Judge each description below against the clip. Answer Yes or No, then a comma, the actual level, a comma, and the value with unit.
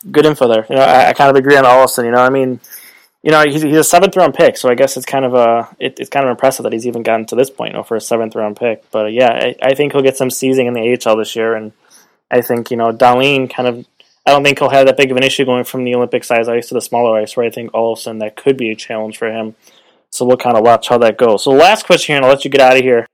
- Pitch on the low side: Yes, low, 125 Hz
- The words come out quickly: Yes, fast, 320 wpm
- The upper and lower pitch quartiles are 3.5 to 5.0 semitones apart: No, average, 2.8 semitones